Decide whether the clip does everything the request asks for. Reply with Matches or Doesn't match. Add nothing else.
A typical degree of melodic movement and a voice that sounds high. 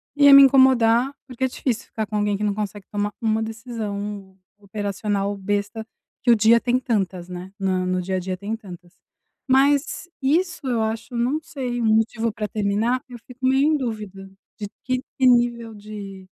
Matches